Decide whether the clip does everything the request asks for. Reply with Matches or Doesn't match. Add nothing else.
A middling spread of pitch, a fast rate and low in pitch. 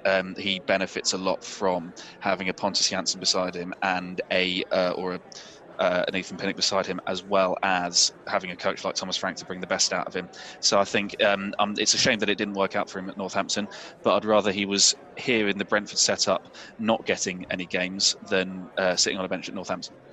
Doesn't match